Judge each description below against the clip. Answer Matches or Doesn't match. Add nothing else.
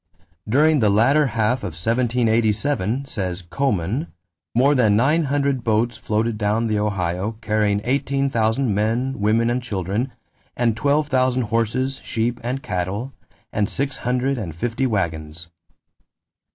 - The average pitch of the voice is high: Doesn't match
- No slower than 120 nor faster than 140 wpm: Matches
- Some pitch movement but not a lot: Matches